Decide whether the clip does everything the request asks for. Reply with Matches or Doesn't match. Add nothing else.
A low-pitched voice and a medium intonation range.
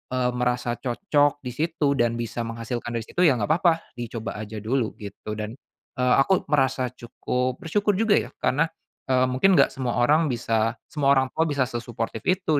Matches